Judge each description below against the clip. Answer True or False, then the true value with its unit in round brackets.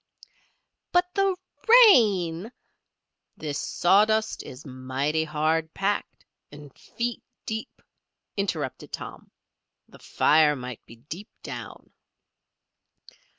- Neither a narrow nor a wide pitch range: False (6.9 semitones)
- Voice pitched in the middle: True (165 Hz)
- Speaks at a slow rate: True (90 wpm)